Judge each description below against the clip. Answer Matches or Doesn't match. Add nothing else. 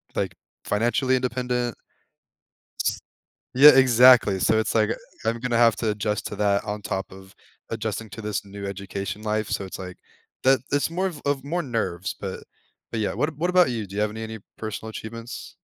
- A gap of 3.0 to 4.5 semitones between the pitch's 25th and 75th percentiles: Matches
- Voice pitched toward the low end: Matches